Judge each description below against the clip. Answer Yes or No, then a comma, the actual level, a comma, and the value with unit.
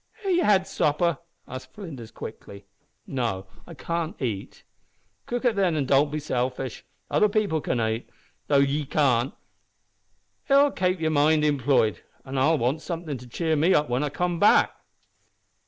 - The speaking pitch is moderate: Yes, medium, 150 Hz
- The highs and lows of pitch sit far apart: No, average, 4.9 semitones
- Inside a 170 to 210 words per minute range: No, average, 160 wpm